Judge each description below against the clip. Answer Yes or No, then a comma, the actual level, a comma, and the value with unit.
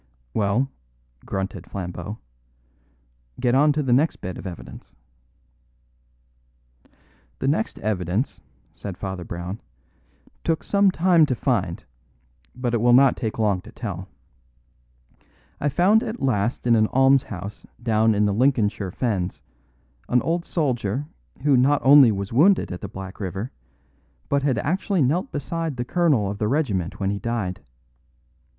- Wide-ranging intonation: Yes, wide, 6.3 semitones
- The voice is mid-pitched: No, low, 120 Hz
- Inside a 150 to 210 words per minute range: No, average, 140 wpm